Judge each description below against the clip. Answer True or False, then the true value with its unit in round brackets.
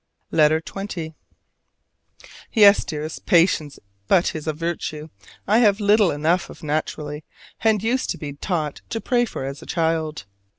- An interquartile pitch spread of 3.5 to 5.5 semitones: True (4.9 semitones)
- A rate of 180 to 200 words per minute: False (155 wpm)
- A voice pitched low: False (165 Hz)